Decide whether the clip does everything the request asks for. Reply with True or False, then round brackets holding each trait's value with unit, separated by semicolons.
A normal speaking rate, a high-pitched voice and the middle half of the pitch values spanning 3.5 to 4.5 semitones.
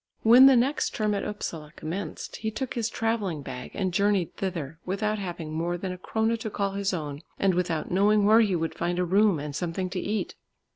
False (210 wpm; 195 Hz; 3.9 semitones)